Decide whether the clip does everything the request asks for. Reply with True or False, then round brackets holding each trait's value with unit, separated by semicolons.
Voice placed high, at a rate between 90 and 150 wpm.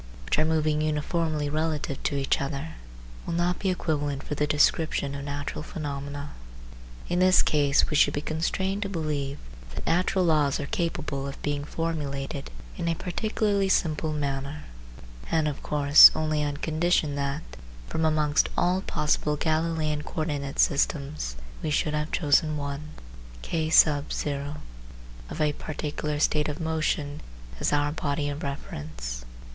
False (150 Hz; 145 wpm)